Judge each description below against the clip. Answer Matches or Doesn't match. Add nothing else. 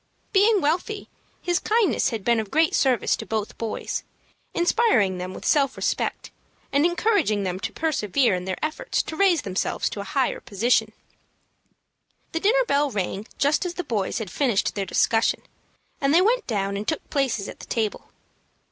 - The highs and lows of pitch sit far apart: Matches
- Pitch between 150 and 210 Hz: Doesn't match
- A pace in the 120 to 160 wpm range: Doesn't match